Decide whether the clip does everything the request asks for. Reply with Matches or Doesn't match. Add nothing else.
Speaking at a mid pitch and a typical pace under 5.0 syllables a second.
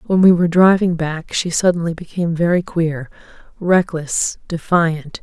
Matches